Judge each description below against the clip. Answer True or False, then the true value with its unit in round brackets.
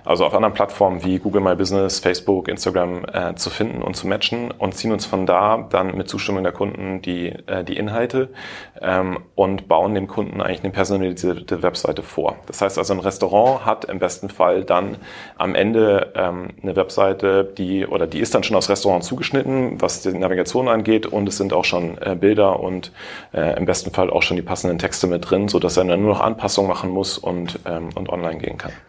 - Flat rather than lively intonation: True (1.9 semitones)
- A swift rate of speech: True (210 wpm)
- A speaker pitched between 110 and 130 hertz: False (95 Hz)